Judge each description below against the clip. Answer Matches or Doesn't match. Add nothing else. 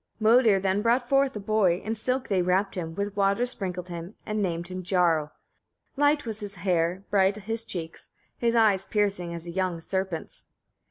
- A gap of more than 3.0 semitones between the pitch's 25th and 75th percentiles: Matches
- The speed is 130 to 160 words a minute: Doesn't match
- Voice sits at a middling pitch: Doesn't match